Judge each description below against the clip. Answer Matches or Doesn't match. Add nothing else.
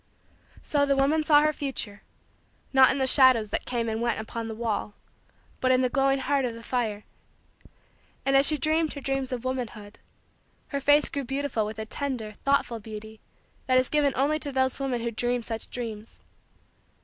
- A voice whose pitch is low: Doesn't match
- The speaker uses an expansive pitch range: Doesn't match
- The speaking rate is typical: Matches